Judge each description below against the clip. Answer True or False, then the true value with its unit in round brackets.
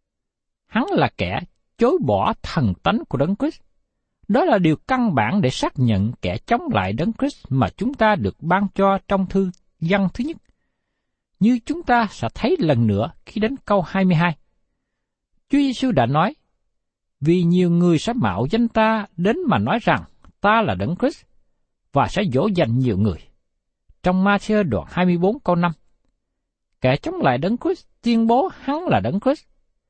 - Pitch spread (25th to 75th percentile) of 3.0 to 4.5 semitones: False (5.6 semitones)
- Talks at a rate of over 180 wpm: False (175 wpm)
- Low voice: False (195 Hz)